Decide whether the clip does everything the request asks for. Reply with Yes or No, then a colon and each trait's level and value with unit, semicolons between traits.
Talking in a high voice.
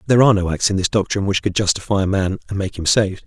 No: low, 100 Hz